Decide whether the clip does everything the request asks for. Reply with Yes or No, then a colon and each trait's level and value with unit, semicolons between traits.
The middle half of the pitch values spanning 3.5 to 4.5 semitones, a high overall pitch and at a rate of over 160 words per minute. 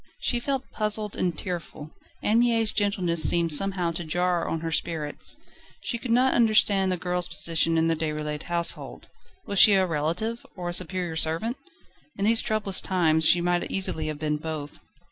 No: average, 4.2 semitones; medium, 175 Hz; average, 175 wpm